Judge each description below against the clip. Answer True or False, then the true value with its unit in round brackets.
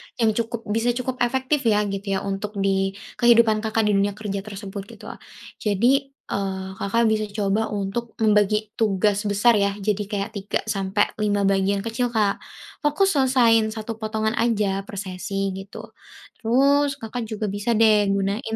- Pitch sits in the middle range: False (215 Hz)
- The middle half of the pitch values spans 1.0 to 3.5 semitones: True (2.5 semitones)